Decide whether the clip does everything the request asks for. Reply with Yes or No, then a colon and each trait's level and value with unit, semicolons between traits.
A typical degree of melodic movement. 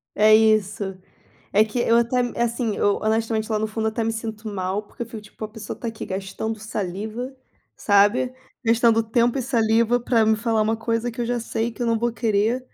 No: narrow, 1.5 semitones